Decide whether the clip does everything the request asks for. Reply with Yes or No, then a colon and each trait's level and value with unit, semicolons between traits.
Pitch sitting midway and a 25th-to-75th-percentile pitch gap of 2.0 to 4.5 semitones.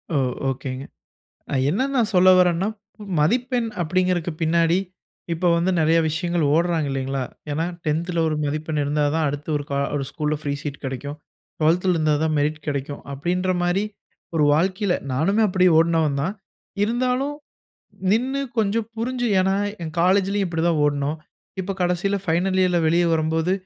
Yes: medium, 170 Hz; average, 3.7 semitones